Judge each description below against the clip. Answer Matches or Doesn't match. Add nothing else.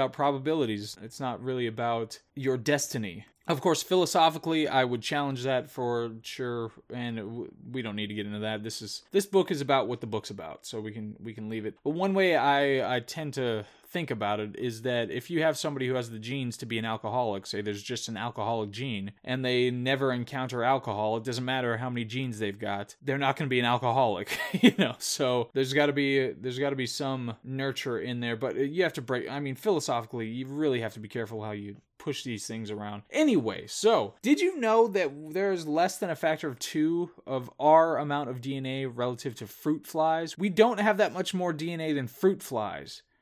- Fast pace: Matches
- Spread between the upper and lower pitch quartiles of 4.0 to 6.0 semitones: Matches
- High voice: Doesn't match